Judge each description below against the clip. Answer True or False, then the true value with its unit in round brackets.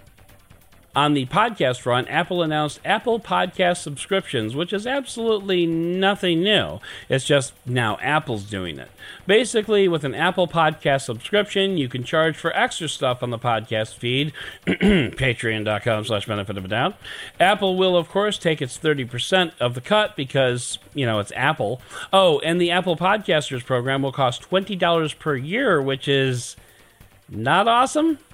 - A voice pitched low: False (150 Hz)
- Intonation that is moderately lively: False (7.4 semitones)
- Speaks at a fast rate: False (150 wpm)